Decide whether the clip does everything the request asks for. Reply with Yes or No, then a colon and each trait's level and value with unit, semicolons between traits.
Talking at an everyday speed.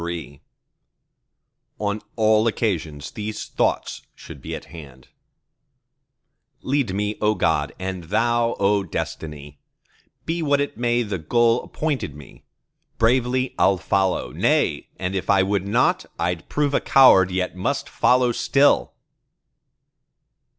No: slow, 125 wpm